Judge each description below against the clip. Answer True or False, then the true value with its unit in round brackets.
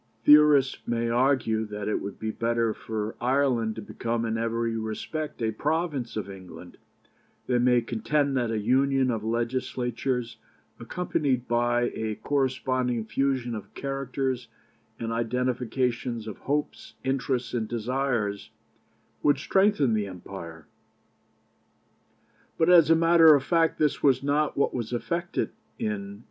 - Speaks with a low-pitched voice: True (125 Hz)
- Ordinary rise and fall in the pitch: True (3.5 semitones)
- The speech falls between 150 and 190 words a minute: False (135 wpm)